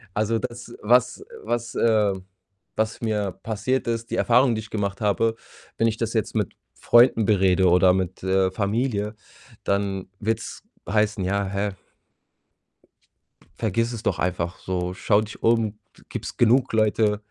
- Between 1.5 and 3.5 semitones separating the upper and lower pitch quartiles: Yes, narrow, 2.6 semitones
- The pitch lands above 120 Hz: No, low, 110 Hz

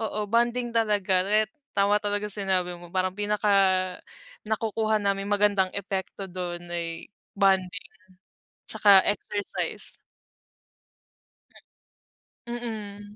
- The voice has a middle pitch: No, high, 205 Hz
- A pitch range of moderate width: No, narrow, 2.0 semitones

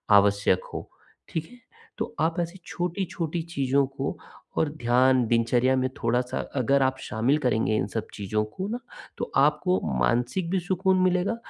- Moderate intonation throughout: No, wide, 6.6 semitones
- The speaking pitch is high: No, low, 135 Hz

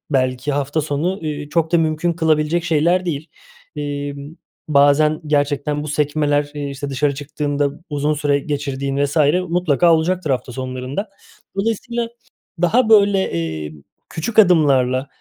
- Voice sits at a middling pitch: Yes, medium, 150 Hz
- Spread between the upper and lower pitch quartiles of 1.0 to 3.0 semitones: Yes, average, 2.7 semitones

